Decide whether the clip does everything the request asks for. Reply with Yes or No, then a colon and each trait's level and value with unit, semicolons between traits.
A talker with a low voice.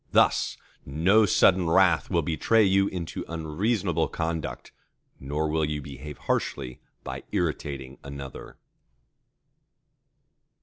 Yes: very low, 80 Hz